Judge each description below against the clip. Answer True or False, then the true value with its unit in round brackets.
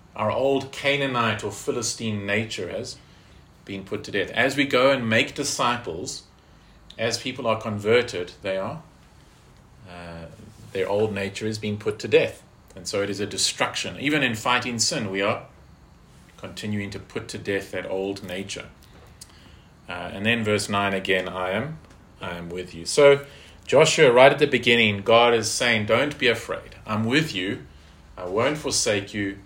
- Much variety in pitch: False (3.8 semitones)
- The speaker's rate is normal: True (170 wpm)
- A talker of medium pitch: False (110 Hz)